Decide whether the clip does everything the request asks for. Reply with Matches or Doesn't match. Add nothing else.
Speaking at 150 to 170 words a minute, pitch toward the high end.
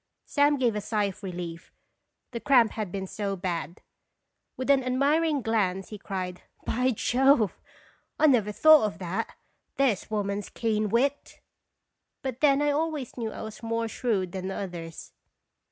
Matches